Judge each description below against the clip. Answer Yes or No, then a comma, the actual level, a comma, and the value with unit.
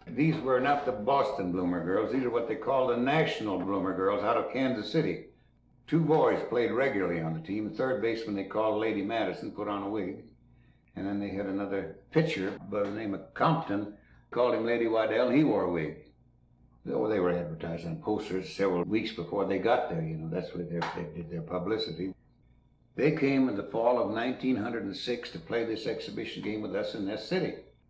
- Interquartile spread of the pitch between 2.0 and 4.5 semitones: No, average, 5.3 semitones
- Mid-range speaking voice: No, low, 105 Hz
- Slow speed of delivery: No, average, 200 wpm